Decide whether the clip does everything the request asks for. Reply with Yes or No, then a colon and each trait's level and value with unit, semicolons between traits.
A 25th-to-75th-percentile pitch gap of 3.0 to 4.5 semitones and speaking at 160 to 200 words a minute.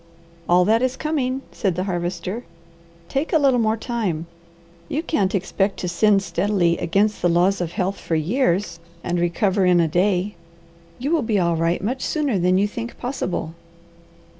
No: average, 5.2 semitones; average, 170 wpm